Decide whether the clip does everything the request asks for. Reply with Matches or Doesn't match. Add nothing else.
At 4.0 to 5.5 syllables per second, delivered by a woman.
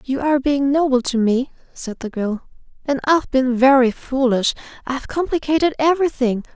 Matches